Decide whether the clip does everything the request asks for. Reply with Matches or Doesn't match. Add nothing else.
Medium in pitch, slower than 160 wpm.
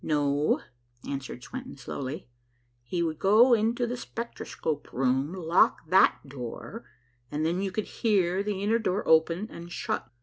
Matches